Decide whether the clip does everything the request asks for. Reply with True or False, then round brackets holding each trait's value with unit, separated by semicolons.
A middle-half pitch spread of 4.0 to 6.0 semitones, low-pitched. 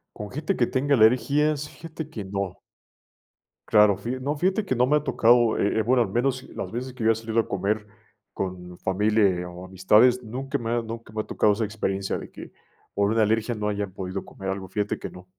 True (4.3 semitones; 110 Hz)